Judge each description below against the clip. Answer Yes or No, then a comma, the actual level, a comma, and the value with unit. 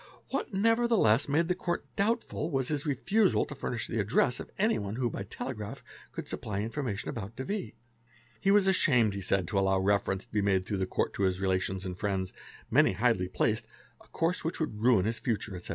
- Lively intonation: Yes, wide, 8.4 semitones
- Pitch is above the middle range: No, low, 115 Hz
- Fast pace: Yes, fast, 210 wpm